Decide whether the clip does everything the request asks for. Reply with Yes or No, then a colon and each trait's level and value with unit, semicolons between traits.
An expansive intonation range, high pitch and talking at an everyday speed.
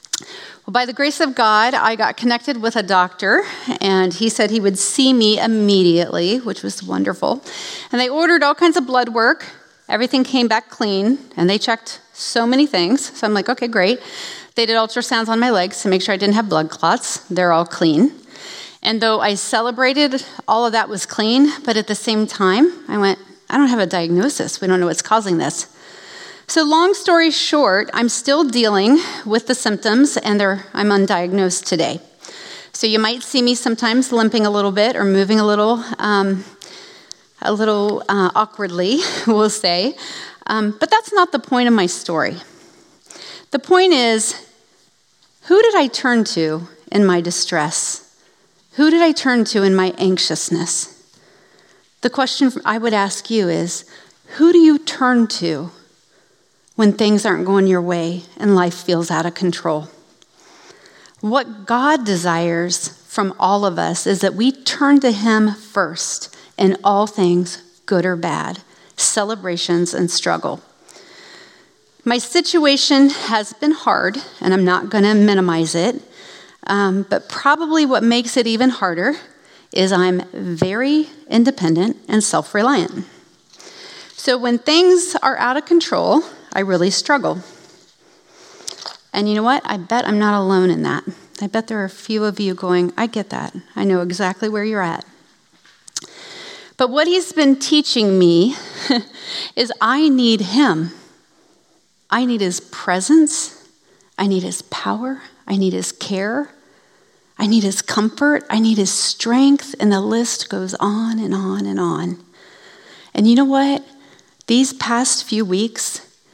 Yes: wide, 6.0 semitones; high, 220 Hz; average, 160 wpm